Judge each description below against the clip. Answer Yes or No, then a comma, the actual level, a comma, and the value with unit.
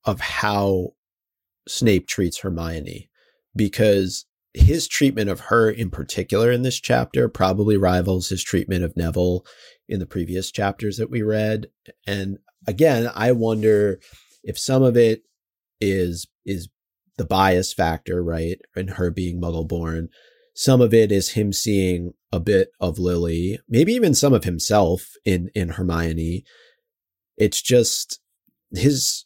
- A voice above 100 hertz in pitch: No, very low, 95 Hz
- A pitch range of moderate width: Yes, average, 4.1 semitones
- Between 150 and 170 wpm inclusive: No, average, 140 wpm